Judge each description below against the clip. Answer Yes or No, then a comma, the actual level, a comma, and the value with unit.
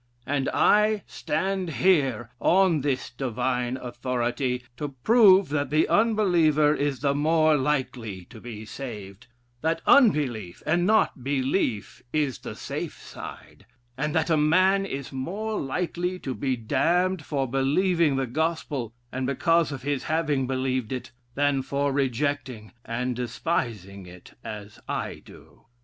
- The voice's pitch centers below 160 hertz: Yes, medium, 140 Hz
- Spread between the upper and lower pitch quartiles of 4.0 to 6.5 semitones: Yes, average, 4.7 semitones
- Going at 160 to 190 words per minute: No, slow, 135 wpm